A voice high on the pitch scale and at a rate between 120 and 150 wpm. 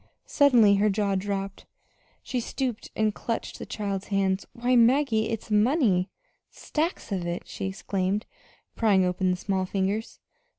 Yes: high, 205 Hz; average, 140 wpm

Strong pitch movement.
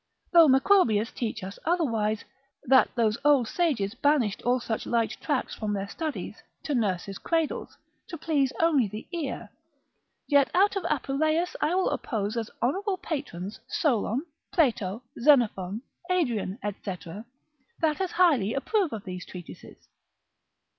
Yes: wide, 7.0 semitones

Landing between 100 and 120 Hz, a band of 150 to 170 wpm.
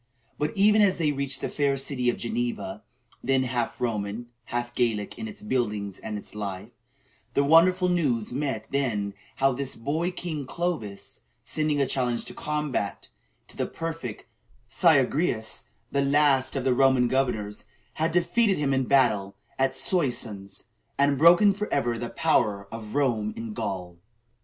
No: low, 135 Hz; average, 155 wpm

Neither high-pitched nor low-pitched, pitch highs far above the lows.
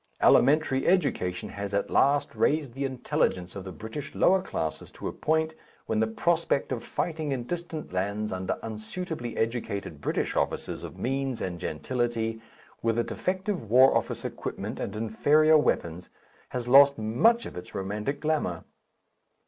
No: low, 120 Hz; wide, 6.5 semitones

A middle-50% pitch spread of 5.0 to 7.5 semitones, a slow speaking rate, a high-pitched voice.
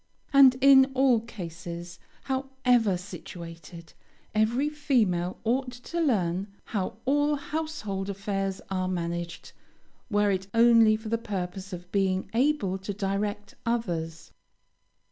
Yes: average, 5.3 semitones; slow, 115 wpm; high, 205 Hz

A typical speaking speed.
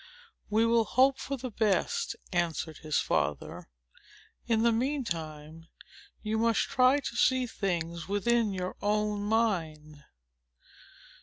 No: slow, 125 wpm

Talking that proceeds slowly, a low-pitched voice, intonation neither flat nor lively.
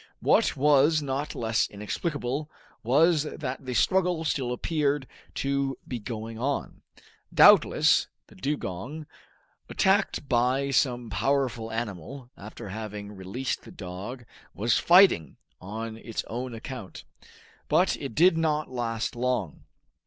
Yes: slow, 120 wpm; low, 125 Hz; average, 4.4 semitones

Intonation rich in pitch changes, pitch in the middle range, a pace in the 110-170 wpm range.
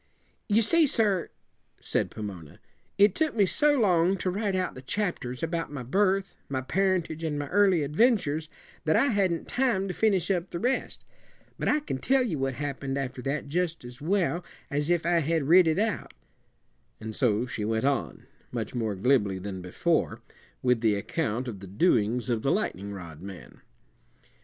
No: wide, 7.8 semitones; medium, 155 Hz; average, 180 wpm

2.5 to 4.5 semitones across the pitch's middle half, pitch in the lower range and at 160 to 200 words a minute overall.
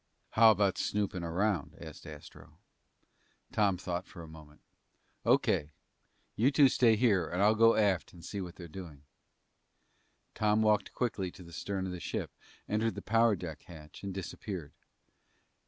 No: average, 3.9 semitones; very low, 95 Hz; average, 150 wpm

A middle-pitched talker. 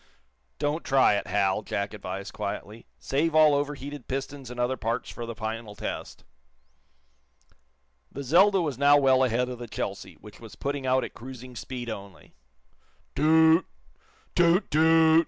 No: low, 130 Hz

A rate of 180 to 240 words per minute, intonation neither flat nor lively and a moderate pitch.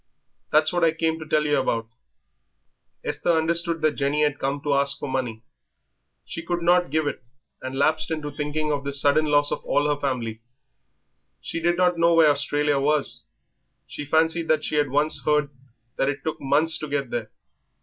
No: average, 190 wpm; narrow, 2.2 semitones; medium, 150 Hz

